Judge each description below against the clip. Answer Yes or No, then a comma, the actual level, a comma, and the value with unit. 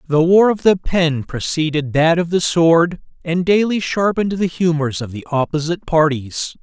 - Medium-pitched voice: Yes, medium, 165 Hz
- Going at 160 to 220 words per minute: Yes, average, 170 wpm